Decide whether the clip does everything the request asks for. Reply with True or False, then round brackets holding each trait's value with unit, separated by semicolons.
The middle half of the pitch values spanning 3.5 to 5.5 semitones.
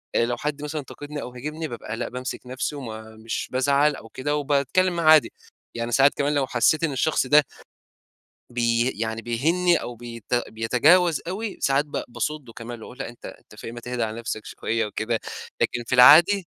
True (4.2 semitones)